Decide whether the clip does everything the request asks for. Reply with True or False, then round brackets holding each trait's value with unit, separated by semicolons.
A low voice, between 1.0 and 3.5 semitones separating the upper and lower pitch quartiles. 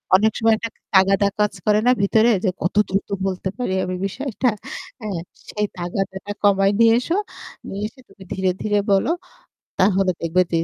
False (200 Hz; 2.5 semitones)